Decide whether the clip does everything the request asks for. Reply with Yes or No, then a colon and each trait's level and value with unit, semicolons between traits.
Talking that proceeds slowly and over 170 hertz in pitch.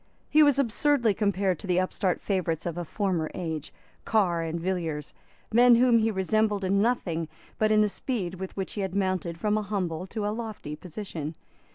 No: average, 190 wpm; high, 190 Hz